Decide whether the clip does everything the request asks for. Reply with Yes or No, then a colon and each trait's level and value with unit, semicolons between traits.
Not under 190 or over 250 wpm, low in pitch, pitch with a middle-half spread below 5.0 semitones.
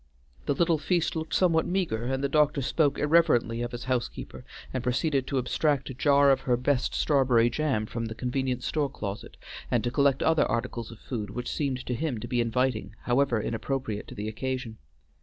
Yes: average, 195 wpm; low, 130 Hz; average, 3.2 semitones